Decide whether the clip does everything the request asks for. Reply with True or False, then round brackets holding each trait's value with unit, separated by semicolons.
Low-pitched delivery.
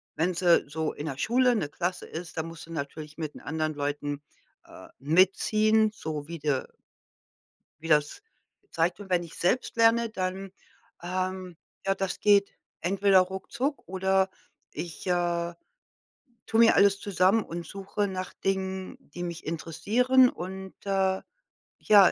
False (185 Hz)